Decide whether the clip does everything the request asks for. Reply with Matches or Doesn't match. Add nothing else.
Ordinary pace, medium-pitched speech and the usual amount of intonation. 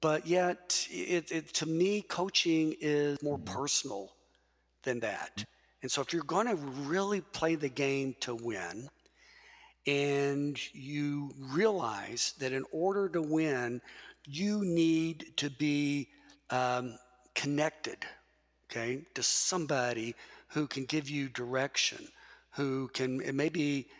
Doesn't match